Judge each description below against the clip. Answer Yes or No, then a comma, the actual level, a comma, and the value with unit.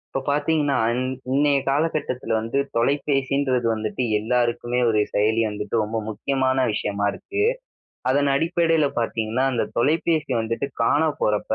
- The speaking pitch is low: Yes, low, 130 Hz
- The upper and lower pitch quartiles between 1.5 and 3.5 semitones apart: No, average, 4.1 semitones